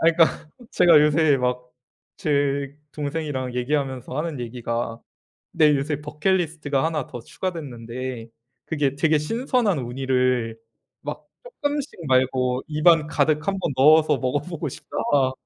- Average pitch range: Yes, average, 3.8 semitones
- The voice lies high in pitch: No, medium, 145 Hz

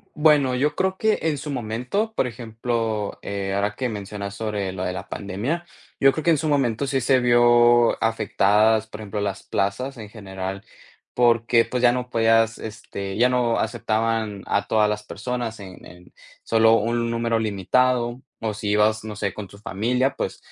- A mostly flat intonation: No, average, 3.1 semitones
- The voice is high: No, low, 115 Hz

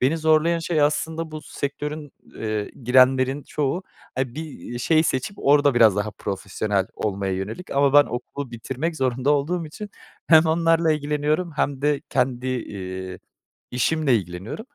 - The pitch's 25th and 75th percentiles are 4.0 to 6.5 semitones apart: Yes, average, 4.8 semitones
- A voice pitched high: No, medium, 140 Hz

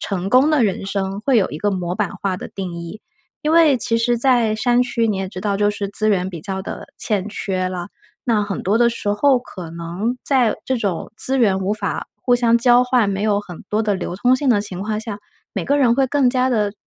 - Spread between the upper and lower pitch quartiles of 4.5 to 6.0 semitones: No, average, 4.1 semitones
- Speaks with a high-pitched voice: Yes, high, 210 Hz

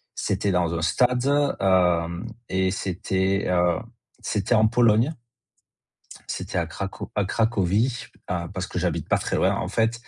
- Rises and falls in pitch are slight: No, average, 4.1 semitones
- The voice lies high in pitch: No, very low, 95 Hz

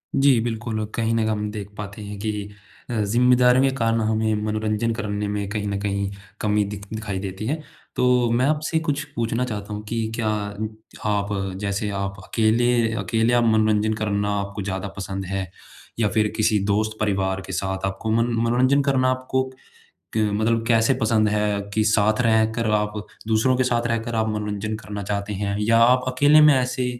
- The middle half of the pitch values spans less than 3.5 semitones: Yes, narrow, 2.4 semitones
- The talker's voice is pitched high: No, low, 110 Hz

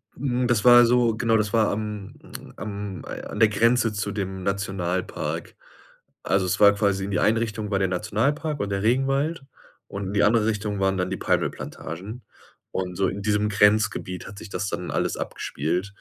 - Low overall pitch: Yes, low, 105 Hz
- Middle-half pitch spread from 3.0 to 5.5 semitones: No, narrow, 2.6 semitones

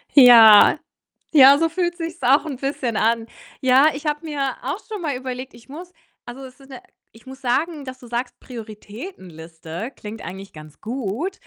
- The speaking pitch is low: No, very high, 260 Hz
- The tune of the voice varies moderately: Yes, average, 4.5 semitones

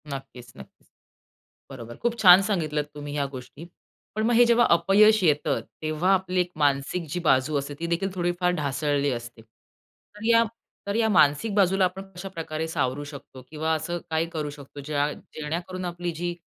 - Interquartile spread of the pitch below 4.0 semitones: No, average, 4.3 semitones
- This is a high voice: No, medium, 160 Hz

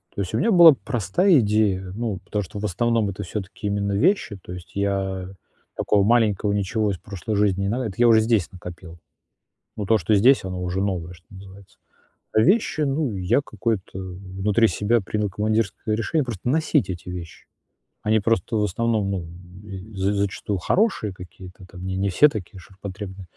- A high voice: No, low, 100 Hz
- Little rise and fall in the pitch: No, average, 3.1 semitones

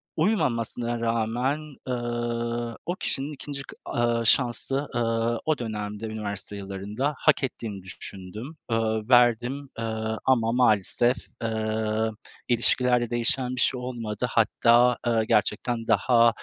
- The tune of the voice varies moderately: No, narrow, 2.1 semitones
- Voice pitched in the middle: No, low, 120 Hz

